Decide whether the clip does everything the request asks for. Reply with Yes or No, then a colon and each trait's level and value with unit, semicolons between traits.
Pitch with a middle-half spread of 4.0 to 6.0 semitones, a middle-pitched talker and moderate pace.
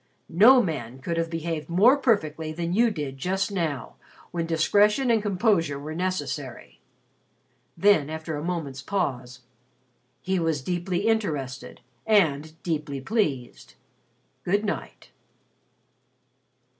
No: average, 5.2 semitones; medium, 165 Hz; slow, 115 wpm